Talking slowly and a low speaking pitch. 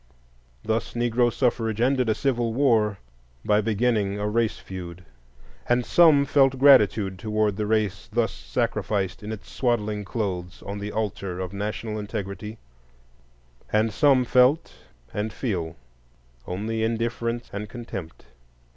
Yes: slow, 130 wpm; low, 110 Hz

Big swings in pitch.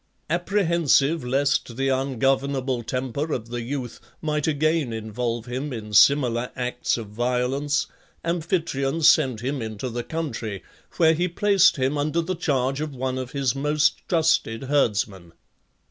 No: average, 4.0 semitones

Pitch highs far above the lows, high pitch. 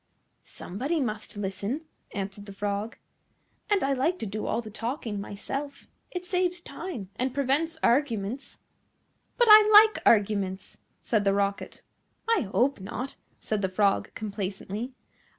Yes: wide, 6.4 semitones; high, 230 Hz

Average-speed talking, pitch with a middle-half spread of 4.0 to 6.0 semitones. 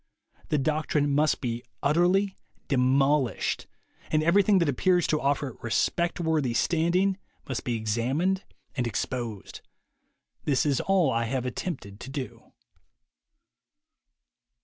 No: slow, 120 wpm; average, 5.2 semitones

